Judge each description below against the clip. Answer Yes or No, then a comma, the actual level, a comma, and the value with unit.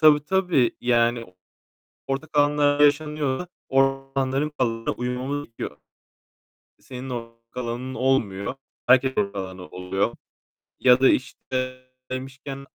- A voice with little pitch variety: No, average, 3.3 semitones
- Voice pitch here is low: Yes, low, 130 Hz